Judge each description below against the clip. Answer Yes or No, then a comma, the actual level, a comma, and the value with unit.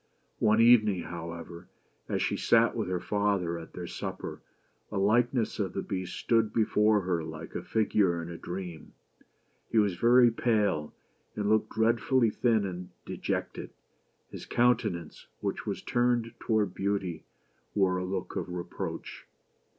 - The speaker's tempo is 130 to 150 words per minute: Yes, average, 145 wpm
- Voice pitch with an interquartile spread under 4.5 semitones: Yes, average, 4.0 semitones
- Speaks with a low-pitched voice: Yes, low, 100 Hz